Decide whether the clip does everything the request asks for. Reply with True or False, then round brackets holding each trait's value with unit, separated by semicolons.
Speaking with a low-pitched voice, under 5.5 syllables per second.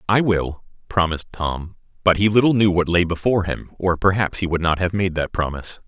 False (90 Hz; 5.7 syllables/s)